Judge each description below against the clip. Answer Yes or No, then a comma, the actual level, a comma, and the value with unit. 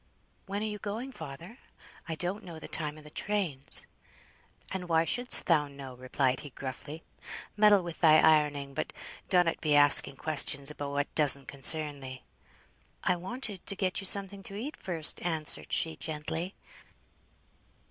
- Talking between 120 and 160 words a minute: Yes, average, 155 wpm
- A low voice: No, medium, 160 Hz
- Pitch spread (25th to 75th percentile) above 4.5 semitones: Yes, average, 4.9 semitones